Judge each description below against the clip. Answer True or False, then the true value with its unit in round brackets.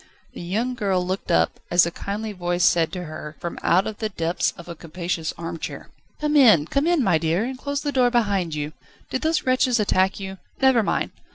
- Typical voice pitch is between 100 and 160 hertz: False (190 Hz)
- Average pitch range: False (6.1 semitones)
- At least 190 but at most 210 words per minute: True (205 wpm)